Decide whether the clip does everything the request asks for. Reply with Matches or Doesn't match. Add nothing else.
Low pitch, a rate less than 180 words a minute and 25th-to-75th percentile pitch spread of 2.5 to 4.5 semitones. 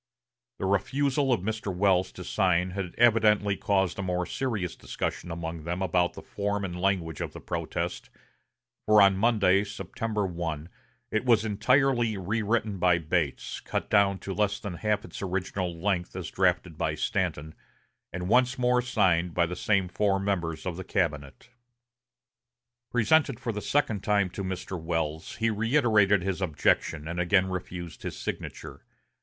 Matches